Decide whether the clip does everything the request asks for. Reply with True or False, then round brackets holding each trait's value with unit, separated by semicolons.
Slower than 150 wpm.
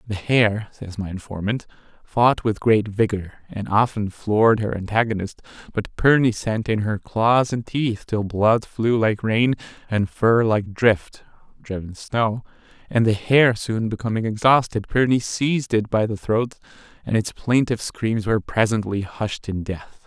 False (160 wpm)